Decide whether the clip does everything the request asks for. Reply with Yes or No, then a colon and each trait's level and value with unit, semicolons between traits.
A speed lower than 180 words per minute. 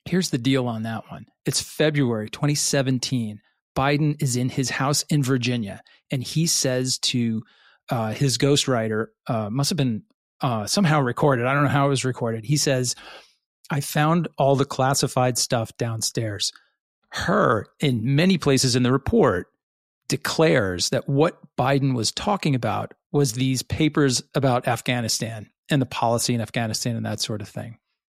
Yes: average, 160 wpm